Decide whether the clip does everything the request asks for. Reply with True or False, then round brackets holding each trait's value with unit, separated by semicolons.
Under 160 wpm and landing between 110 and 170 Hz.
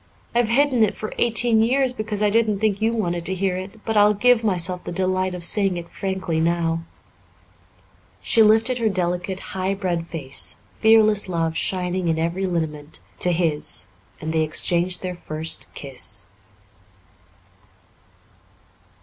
False (150 wpm; 185 Hz)